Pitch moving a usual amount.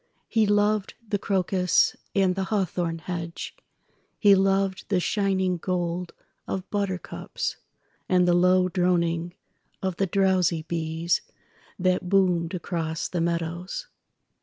No: narrow, 2.2 semitones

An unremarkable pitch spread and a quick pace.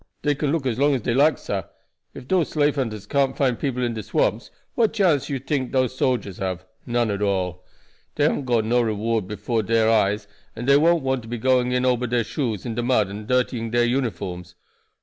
Yes: average, 3.7 semitones; fast, 220 wpm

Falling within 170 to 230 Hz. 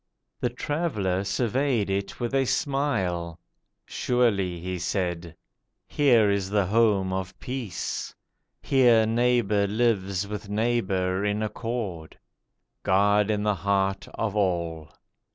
No: low, 100 Hz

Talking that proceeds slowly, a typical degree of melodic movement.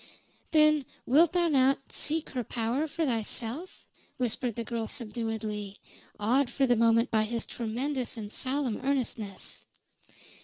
Yes: slow, 130 wpm; average, 3.9 semitones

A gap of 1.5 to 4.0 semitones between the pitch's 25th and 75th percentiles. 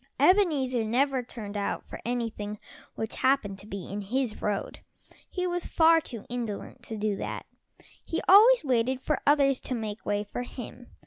No: average, 4.7 semitones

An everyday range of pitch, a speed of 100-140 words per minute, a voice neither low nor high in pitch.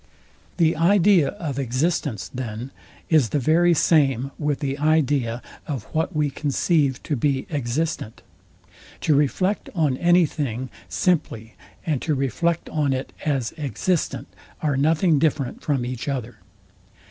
Yes: average, 3.6 semitones; slow, 135 wpm; medium, 145 Hz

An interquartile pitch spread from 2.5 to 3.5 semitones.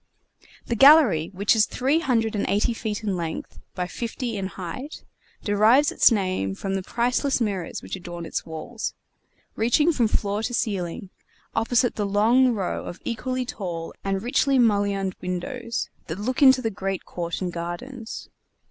No: average, 4.7 semitones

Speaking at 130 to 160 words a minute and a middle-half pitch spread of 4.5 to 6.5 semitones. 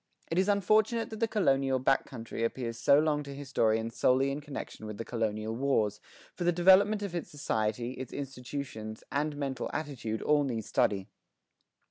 No: average, 170 wpm; average, 5.1 semitones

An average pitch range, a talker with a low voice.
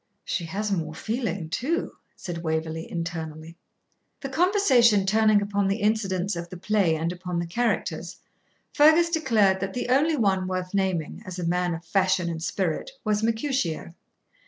No: average, 4.6 semitones; high, 190 Hz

